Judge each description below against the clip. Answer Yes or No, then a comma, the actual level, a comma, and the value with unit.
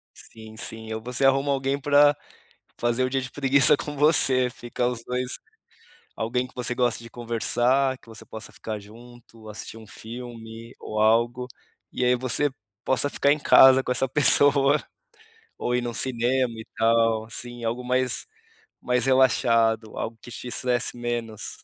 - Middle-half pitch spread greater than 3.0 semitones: No, narrow, 2.4 semitones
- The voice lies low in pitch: Yes, low, 120 Hz